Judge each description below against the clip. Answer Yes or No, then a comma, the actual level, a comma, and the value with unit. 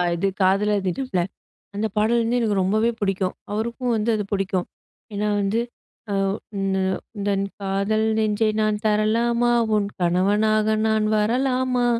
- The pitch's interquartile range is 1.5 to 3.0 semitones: Yes, narrow, 2.5 semitones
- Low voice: No, high, 210 Hz